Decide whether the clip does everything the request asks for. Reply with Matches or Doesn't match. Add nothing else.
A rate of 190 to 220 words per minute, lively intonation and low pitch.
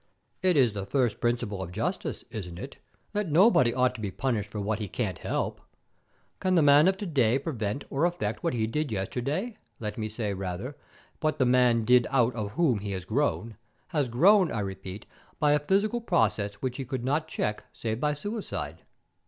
Matches